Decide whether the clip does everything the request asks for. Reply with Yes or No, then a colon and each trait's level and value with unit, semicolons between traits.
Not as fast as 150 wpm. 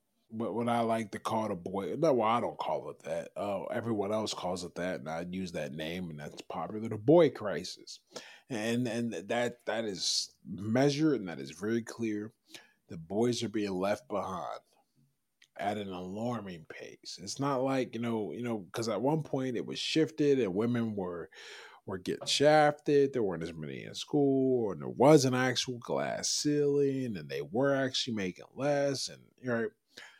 No: average, 190 wpm